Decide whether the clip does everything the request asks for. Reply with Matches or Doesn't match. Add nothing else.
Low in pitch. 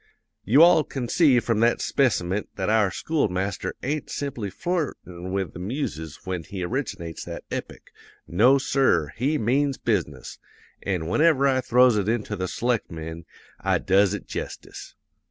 Matches